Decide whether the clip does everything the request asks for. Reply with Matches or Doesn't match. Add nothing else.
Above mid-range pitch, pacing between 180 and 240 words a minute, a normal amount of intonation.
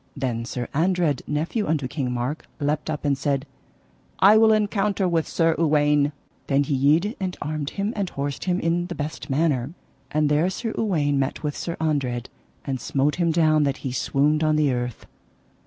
Doesn't match